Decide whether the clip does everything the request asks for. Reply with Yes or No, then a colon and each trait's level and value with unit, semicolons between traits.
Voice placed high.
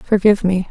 Yes: high, 195 Hz